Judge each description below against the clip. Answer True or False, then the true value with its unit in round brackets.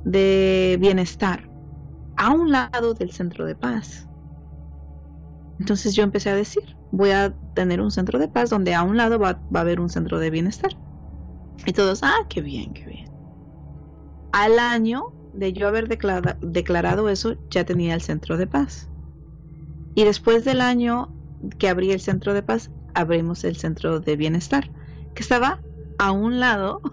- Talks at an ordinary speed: True (165 wpm)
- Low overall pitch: False (185 Hz)